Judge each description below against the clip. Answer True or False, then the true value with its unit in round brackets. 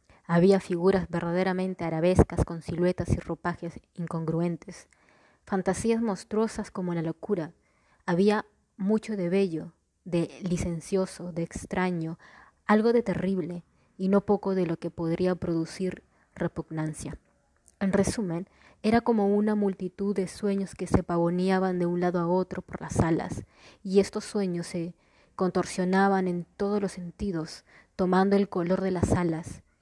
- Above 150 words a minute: False (135 wpm)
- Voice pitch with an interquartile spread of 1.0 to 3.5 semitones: True (2.5 semitones)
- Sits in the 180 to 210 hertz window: True (185 Hz)